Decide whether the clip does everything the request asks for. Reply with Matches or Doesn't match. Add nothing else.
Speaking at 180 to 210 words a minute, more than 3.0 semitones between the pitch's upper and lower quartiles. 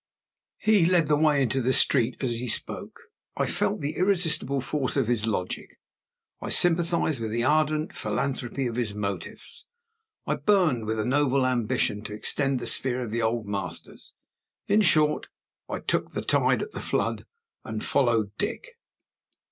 Doesn't match